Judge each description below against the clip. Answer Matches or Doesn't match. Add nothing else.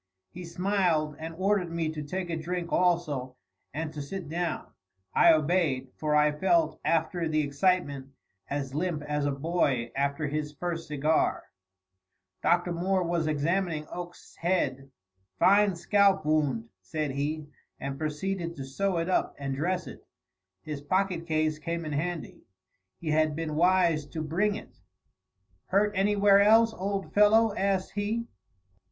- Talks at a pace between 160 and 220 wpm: Doesn't match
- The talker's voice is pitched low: Doesn't match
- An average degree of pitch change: Matches